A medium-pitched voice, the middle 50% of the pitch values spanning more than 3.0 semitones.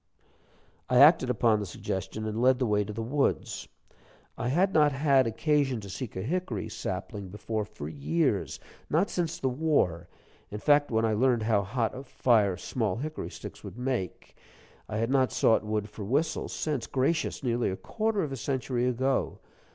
No: low, 125 Hz; average, 4.7 semitones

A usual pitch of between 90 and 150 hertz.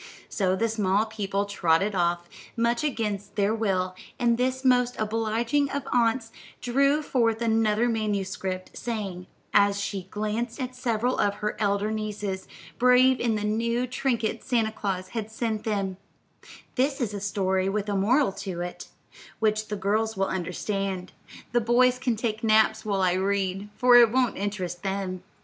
No: high, 215 Hz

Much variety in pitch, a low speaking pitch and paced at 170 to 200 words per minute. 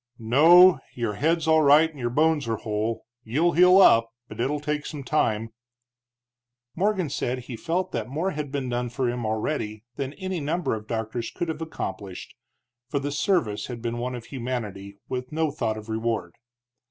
Yes: wide, 5.7 semitones; low, 130 Hz; average, 180 wpm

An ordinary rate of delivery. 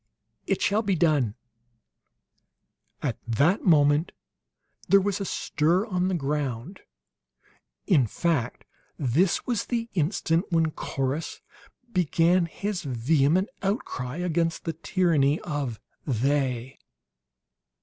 No: slow, 105 wpm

